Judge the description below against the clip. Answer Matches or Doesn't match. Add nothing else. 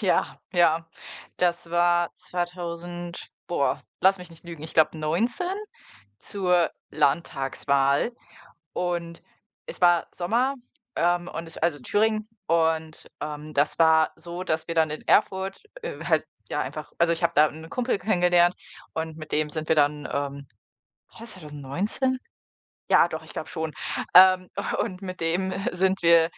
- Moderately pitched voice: Matches